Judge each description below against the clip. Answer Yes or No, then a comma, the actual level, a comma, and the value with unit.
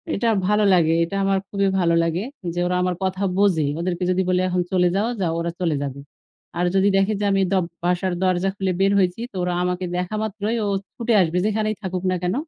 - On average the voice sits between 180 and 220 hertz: Yes, medium, 185 Hz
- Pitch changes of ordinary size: No, narrow, 2.1 semitones